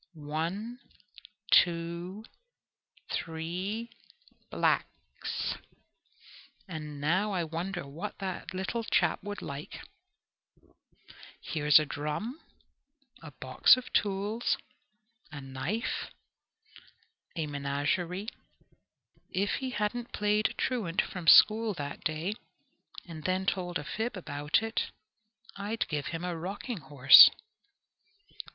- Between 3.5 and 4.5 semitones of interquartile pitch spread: No, average, 5.3 semitones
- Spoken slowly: Yes, slow, 95 wpm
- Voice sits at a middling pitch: Yes, medium, 180 Hz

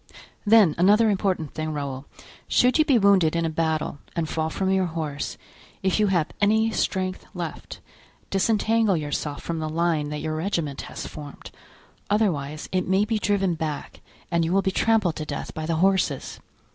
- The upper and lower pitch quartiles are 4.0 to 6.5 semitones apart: Yes, average, 4.3 semitones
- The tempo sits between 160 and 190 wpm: Yes, average, 175 wpm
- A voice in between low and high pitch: Yes, medium, 175 Hz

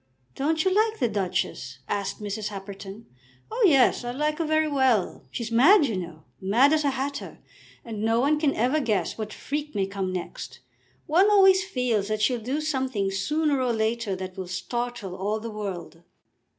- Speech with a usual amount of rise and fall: No, wide, 6.8 semitones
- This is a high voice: Yes, high, 235 Hz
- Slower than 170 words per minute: No, average, 180 wpm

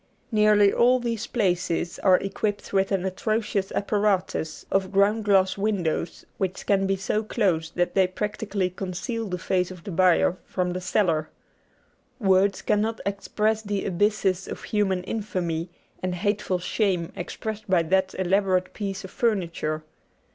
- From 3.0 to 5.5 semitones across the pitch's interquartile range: No, narrow, 2.4 semitones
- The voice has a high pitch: Yes, high, 195 Hz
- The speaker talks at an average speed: Yes, average, 145 wpm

